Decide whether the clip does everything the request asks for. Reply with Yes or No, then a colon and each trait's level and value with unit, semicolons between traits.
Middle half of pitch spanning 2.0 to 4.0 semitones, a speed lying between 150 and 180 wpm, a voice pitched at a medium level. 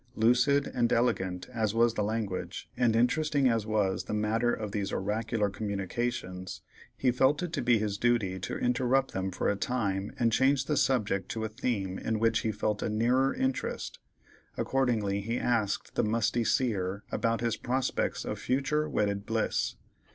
No: average, 3.3 semitones; average, 170 wpm; low, 115 Hz